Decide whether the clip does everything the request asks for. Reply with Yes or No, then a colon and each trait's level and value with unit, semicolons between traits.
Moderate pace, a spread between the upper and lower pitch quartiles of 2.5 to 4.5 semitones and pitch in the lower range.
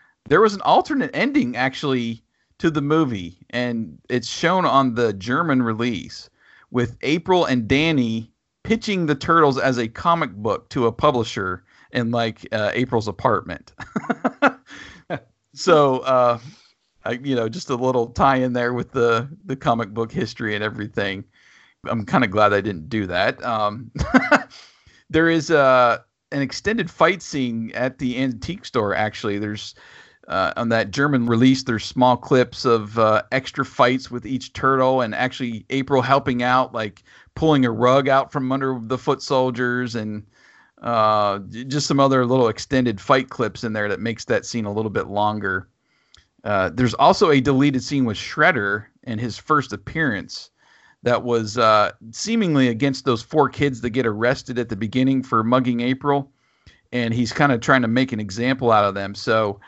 Yes: average, 165 wpm; average, 3.2 semitones; low, 125 Hz